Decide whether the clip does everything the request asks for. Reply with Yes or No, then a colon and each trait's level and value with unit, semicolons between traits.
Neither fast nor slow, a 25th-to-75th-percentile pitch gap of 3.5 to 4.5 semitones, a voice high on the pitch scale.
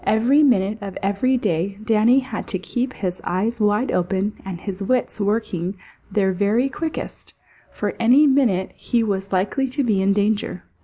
Yes: average, 165 wpm; average, 4.2 semitones; high, 210 Hz